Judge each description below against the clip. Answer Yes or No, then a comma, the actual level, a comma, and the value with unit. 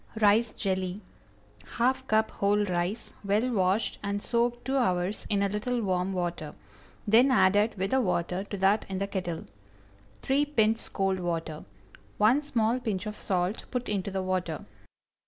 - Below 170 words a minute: Yes, average, 160 wpm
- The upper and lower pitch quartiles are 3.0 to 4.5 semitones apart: Yes, average, 3.6 semitones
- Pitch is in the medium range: No, high, 205 Hz